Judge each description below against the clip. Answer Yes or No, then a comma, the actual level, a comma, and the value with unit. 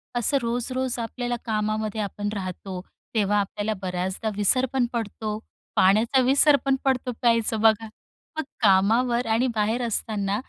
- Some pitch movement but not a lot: Yes, average, 3.0 semitones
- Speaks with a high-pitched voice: Yes, high, 220 Hz